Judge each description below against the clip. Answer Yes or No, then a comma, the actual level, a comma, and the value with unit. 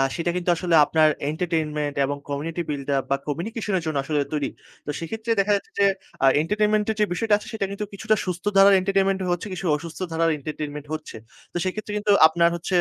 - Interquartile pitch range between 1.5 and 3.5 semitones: No, average, 4.4 semitones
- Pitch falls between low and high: Yes, medium, 175 Hz